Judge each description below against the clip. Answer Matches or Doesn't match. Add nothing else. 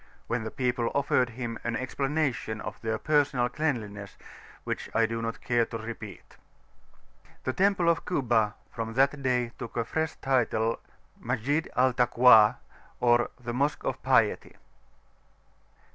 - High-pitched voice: Doesn't match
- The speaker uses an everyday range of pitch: Matches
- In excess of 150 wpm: Doesn't match